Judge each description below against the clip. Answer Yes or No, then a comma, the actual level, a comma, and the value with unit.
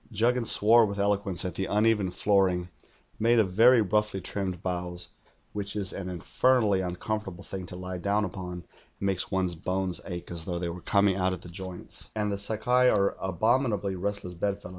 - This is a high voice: No, very low, 95 Hz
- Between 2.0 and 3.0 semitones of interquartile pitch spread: Yes, narrow, 2.6 semitones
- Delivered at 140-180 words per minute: No, average, 195 wpm